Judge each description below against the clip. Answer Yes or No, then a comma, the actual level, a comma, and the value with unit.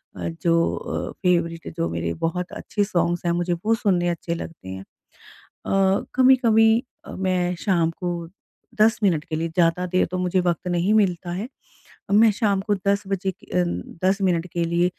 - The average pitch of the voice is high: No, medium, 180 Hz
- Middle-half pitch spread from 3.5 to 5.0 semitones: No, average, 2.7 semitones